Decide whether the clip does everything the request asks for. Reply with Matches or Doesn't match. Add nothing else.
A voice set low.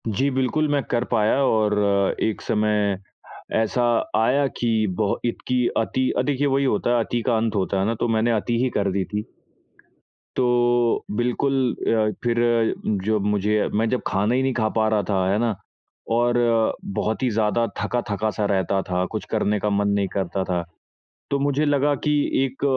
Matches